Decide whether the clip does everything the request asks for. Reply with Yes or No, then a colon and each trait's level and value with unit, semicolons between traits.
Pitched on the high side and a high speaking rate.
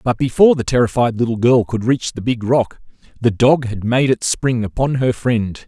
No: low, 120 Hz; fast, 210 wpm